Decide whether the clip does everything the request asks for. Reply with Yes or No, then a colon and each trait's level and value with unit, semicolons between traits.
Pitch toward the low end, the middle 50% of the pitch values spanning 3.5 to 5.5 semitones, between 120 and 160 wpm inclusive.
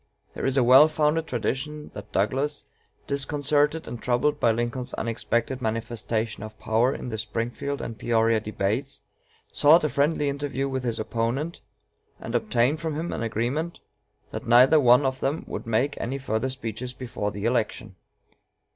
Yes: low, 125 Hz; average, 3.9 semitones; average, 155 wpm